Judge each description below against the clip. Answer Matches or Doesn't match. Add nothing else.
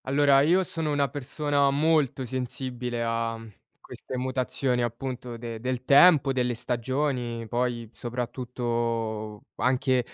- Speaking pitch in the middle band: Doesn't match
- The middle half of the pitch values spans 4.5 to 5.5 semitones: Doesn't match